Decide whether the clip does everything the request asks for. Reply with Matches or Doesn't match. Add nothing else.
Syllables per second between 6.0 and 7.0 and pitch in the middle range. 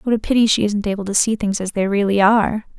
Doesn't match